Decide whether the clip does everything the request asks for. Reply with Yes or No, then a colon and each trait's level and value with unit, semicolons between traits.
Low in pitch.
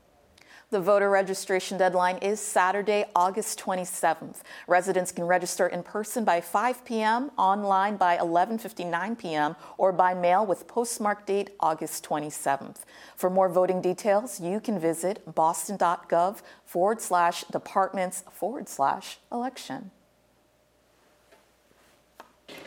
No: medium, 185 Hz